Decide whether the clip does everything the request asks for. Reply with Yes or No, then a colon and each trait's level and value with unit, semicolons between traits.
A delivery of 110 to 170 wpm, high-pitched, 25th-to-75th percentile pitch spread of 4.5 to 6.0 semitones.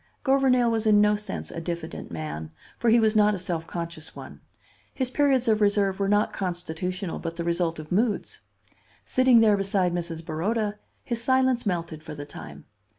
No: average, 180 wpm; high, 195 Hz; average, 5.1 semitones